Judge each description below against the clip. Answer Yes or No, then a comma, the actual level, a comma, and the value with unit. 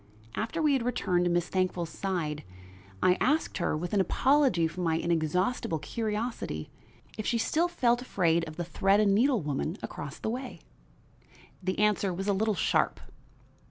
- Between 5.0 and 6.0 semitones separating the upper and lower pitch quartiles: Yes, wide, 5.4 semitones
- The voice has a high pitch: Yes, high, 195 Hz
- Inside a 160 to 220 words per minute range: Yes, average, 165 wpm